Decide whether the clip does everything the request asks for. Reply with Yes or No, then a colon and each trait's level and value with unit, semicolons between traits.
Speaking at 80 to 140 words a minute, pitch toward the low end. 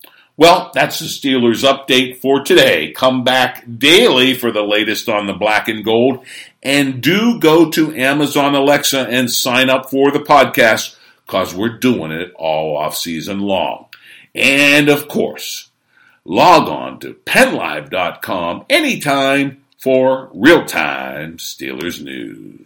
Yes: slow, 135 wpm; low, 130 Hz